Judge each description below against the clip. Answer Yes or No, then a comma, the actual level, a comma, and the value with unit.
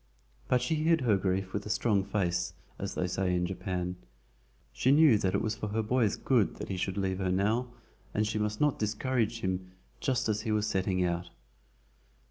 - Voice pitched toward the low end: Yes, low, 105 Hz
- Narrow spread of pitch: No, average, 3.6 semitones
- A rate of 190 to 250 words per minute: Yes, average, 200 wpm